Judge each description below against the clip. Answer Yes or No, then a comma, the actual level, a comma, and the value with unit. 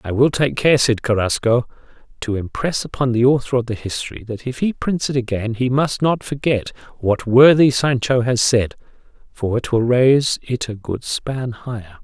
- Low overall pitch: Yes, low, 120 Hz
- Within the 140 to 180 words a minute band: No, average, 190 wpm